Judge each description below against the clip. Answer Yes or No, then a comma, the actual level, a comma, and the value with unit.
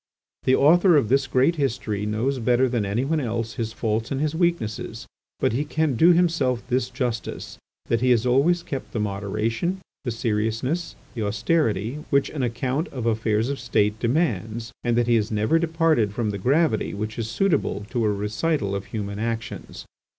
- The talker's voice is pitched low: Yes, low, 120 Hz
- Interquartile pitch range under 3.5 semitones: No, average, 4.7 semitones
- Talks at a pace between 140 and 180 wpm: Yes, average, 175 wpm